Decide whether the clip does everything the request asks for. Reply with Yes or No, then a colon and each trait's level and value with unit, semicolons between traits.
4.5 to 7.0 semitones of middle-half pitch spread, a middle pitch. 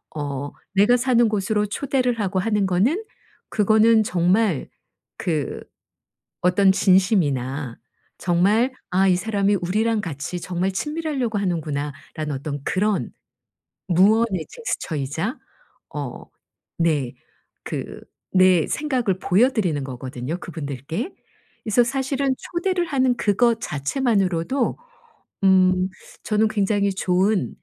No: average, 5.3 semitones; high, 195 Hz